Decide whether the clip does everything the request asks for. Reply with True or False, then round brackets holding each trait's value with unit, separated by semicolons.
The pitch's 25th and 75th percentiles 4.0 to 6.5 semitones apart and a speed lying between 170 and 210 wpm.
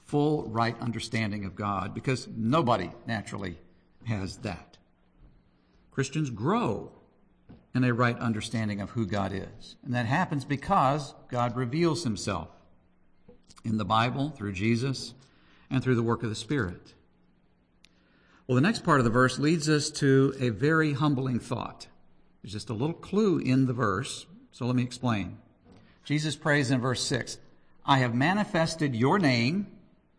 False (5.4 semitones; 150 wpm)